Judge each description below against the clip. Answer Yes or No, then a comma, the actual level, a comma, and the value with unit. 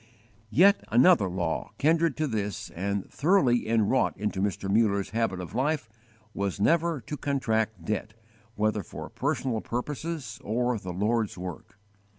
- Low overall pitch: Yes, low, 110 Hz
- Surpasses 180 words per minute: No, average, 140 wpm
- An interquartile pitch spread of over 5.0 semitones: Yes, wide, 5.5 semitones